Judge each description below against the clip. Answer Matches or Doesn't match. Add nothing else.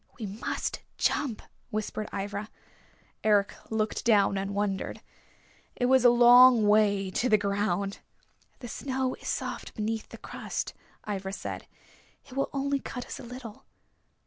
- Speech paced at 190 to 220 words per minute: Doesn't match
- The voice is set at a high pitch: Matches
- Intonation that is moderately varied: Matches